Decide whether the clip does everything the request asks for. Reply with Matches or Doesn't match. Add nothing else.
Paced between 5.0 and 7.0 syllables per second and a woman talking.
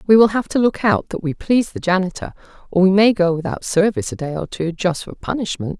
Matches